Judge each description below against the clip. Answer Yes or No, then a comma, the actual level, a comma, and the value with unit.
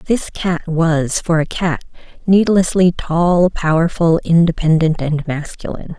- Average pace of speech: No, slow, 120 wpm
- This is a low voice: No, medium, 165 Hz